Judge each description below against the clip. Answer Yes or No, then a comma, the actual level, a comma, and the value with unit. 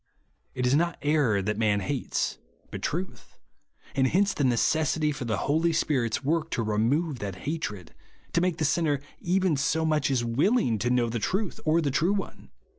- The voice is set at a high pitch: No, medium, 145 Hz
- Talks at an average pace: Yes, average, 190 wpm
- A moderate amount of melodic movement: No, wide, 5.8 semitones